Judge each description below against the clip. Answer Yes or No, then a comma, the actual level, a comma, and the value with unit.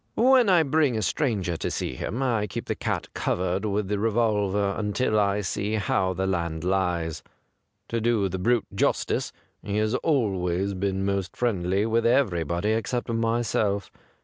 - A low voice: Yes, low, 105 Hz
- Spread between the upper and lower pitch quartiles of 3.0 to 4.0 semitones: Yes, average, 3.6 semitones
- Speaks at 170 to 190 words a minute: No, average, 160 wpm